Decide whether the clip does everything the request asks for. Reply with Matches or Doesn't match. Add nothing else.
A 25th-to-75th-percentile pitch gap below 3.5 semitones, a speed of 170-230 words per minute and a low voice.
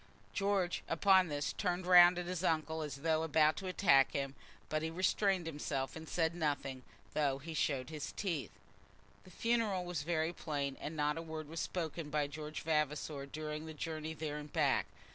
Doesn't match